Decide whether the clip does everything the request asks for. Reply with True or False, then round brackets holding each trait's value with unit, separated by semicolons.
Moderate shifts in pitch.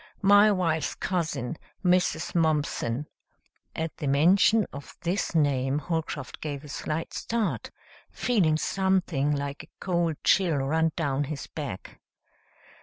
True (4.0 semitones)